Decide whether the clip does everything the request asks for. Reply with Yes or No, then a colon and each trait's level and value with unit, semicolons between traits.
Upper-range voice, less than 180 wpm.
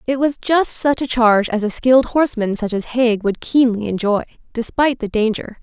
No: high, 235 Hz; fast, 205 wpm